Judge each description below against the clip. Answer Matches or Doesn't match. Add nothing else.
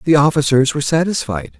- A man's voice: Matches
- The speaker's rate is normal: Matches